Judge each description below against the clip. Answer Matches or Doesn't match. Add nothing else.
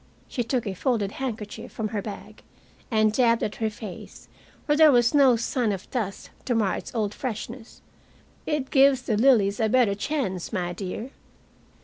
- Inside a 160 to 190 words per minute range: Matches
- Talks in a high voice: Matches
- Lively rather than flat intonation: Doesn't match